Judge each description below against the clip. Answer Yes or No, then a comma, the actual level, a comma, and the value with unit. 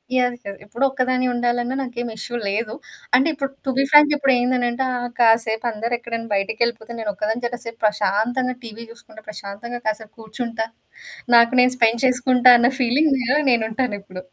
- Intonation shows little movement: Yes, narrow, 2.3 semitones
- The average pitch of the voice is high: Yes, high, 240 Hz